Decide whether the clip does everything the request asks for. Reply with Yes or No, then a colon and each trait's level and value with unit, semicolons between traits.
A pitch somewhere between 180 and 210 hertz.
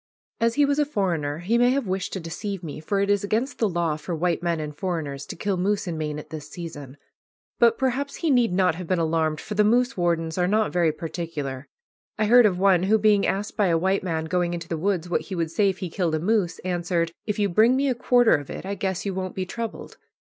Yes: medium, 185 Hz